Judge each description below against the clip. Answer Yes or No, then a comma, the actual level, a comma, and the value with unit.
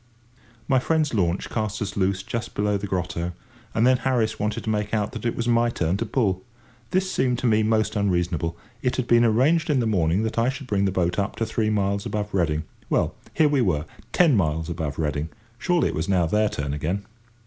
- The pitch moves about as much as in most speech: Yes, average, 4.7 semitones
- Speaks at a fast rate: Yes, fast, 220 wpm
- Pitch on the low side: Yes, low, 105 Hz